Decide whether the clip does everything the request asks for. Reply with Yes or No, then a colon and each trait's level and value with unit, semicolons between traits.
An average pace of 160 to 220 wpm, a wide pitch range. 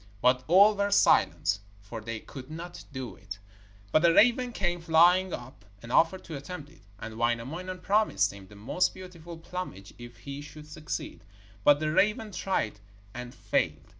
Yes: average, 165 wpm; wide, 7.4 semitones